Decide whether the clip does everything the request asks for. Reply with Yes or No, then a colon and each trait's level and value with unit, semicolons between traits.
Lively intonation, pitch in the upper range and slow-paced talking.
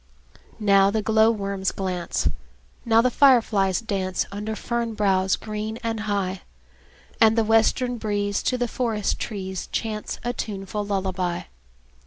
No: narrow, 2.6 semitones; high, 210 Hz; slow, 130 wpm